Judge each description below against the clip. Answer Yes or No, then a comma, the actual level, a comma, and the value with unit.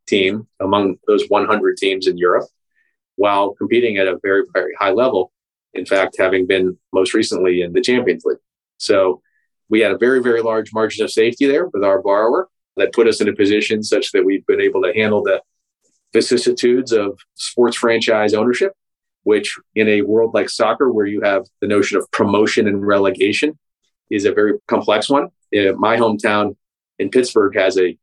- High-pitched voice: No, low, 115 Hz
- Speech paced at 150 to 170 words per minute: No, average, 180 wpm